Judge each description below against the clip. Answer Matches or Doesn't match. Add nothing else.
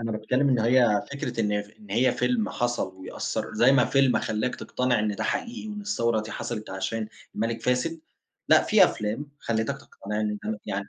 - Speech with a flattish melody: Doesn't match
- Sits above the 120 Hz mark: Doesn't match